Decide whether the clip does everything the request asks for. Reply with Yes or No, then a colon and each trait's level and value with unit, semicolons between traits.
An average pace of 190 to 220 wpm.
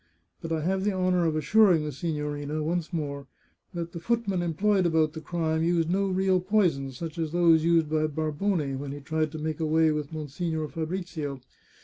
Yes: average, 195 wpm